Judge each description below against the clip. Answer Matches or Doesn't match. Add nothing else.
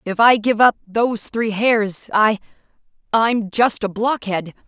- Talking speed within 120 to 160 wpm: Matches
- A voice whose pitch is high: Matches